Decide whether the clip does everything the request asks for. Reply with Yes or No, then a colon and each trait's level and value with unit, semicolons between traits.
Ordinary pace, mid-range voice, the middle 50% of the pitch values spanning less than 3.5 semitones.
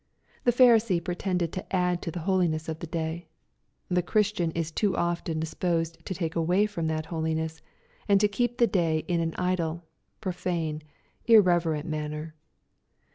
Yes: average, 155 wpm; medium, 170 Hz; narrow, 2.6 semitones